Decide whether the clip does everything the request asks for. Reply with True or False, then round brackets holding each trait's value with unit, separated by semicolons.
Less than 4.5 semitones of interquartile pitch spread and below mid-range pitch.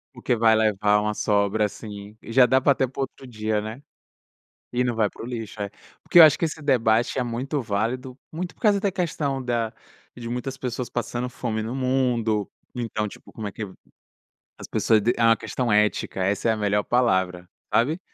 True (3.2 semitones; 115 Hz)